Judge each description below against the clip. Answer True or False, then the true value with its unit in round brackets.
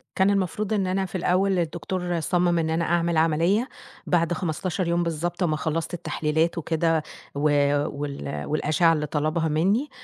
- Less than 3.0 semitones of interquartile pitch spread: True (2.5 semitones)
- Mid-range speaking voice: True (170 Hz)